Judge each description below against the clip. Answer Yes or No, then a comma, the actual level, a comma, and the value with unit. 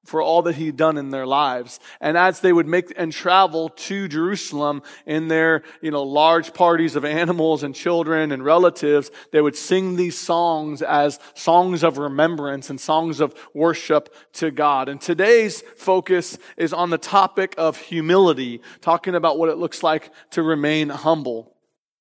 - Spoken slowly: No, average, 170 wpm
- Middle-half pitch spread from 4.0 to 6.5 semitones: No, narrow, 2.6 semitones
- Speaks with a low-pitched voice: No, medium, 160 Hz